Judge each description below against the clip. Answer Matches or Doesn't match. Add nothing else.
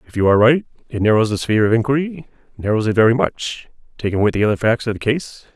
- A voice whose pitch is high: Doesn't match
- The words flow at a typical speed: Doesn't match